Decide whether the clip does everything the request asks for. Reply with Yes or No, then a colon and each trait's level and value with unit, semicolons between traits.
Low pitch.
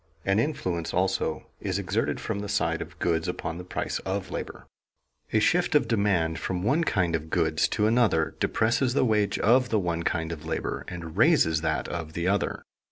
Yes: very low, 95 Hz